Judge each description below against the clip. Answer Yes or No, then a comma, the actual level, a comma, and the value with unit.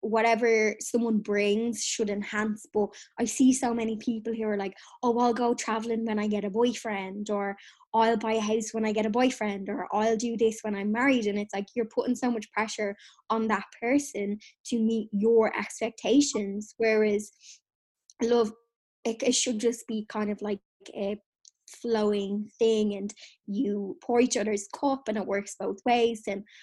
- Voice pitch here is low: No, high, 220 Hz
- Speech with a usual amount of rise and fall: No, narrow, 2.1 semitones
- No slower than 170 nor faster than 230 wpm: Yes, average, 180 wpm